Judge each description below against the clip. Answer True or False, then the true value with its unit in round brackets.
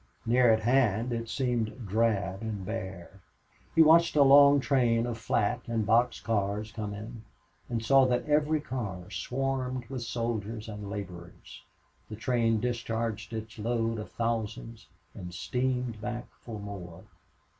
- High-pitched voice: False (115 Hz)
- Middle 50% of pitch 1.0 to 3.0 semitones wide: True (2.7 semitones)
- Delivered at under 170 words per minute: True (145 wpm)